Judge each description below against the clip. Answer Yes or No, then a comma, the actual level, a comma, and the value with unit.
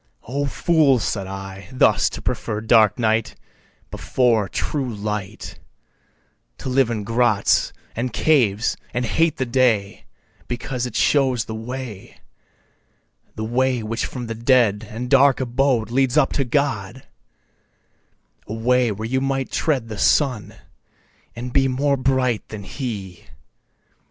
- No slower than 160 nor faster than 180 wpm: No, slow, 135 wpm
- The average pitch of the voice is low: Yes, low, 120 Hz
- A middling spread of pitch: Yes, average, 3.3 semitones